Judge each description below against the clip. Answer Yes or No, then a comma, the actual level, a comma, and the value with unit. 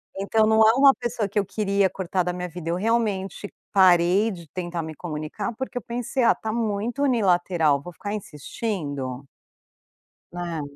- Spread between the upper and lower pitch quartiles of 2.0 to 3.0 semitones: No, average, 4.2 semitones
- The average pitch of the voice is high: Yes, high, 195 Hz